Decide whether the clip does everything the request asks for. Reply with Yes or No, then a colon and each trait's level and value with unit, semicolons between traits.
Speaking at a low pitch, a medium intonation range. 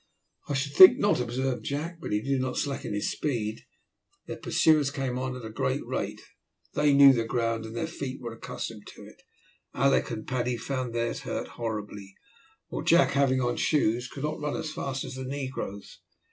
Yes: low, 130 Hz; average, 3.3 semitones